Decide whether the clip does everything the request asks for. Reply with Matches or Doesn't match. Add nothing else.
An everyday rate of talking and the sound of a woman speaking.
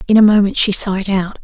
Doesn't match